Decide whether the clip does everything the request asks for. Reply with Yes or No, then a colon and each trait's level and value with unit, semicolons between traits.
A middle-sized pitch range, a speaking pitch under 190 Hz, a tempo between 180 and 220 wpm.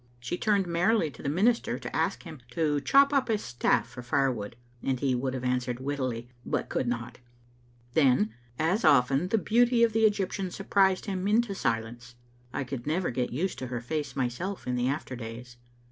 No: wide, 7.7 semitones; medium, 140 Hz; average, 190 wpm